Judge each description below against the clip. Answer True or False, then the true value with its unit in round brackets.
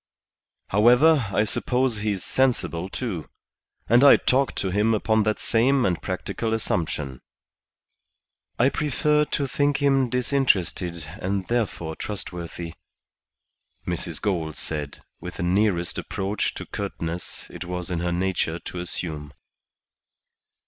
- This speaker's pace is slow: True (120 wpm)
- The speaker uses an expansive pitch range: True (6.1 semitones)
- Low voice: True (100 Hz)